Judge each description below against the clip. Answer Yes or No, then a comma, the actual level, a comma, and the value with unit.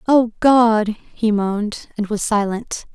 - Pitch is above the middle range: Yes, high, 220 Hz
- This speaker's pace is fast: No, average, 145 wpm